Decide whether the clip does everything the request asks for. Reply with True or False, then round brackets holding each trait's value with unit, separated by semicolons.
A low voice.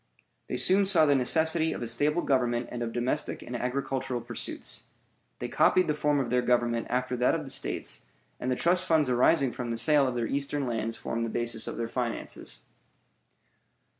True (125 Hz)